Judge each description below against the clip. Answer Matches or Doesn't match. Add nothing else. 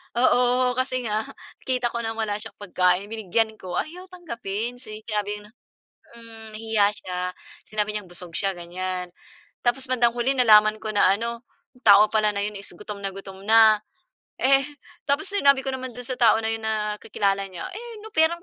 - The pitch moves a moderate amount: Matches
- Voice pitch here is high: Matches